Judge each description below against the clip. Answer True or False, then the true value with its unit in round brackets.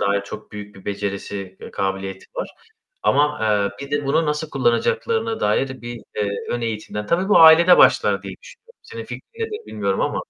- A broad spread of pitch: True (8.3 semitones)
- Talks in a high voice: False (120 Hz)